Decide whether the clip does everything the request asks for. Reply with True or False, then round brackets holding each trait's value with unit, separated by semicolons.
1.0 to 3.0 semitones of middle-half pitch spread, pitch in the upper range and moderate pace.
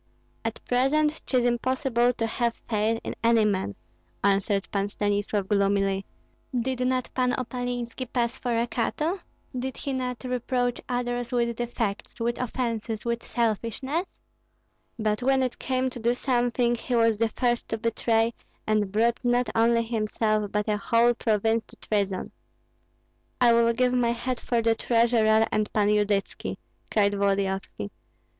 True (2.4 semitones; 235 Hz; 150 wpm)